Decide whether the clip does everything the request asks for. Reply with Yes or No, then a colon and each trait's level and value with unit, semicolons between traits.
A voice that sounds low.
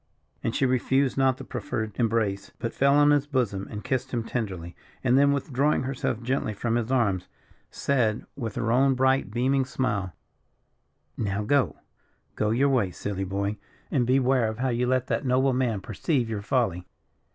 Yes: low, 120 Hz